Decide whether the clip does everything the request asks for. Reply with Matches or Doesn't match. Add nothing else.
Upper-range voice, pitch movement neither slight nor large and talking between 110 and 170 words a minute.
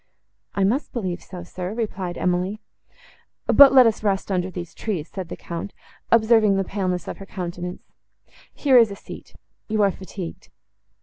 Matches